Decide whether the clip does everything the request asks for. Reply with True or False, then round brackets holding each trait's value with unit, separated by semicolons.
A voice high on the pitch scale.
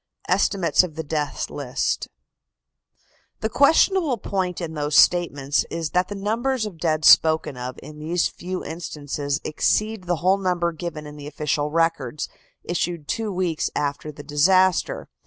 False (165 Hz)